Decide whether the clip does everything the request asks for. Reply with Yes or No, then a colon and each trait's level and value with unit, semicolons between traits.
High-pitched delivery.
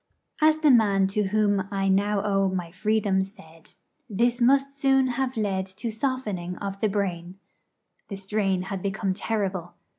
Yes: high, 200 Hz